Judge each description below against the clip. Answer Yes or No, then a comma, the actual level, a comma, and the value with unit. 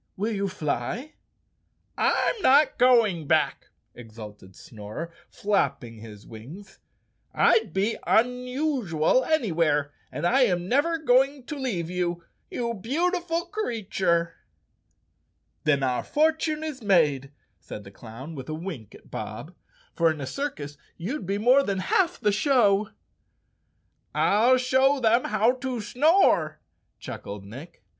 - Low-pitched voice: No, high, 205 Hz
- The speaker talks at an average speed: No, slow, 130 wpm